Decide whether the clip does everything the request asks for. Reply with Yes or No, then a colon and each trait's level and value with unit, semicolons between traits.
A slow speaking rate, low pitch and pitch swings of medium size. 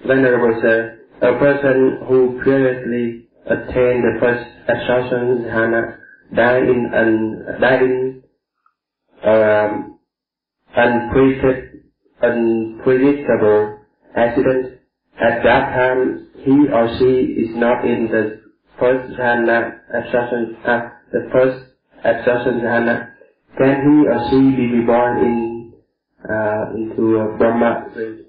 No: slow, 100 wpm; low, 120 Hz; narrow, 2.0 semitones